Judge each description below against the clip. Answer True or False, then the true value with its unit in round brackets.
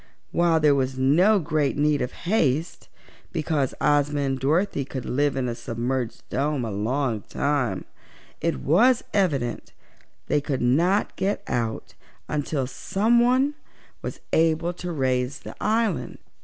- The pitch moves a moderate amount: True (4.8 semitones)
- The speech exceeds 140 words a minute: False (135 wpm)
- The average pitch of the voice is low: False (145 Hz)